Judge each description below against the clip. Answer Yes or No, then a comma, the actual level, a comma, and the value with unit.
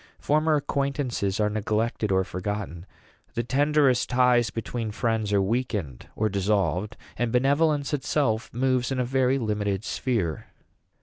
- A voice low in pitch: Yes, low, 115 Hz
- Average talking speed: No, slow, 130 wpm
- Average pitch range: Yes, average, 4.3 semitones